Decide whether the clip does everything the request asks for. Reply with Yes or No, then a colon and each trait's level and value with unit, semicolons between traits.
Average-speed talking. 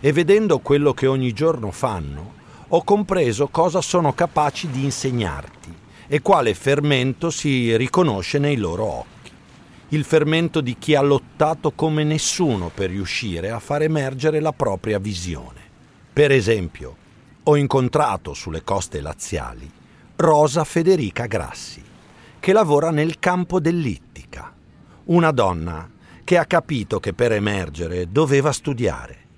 Yes: average, 130 wpm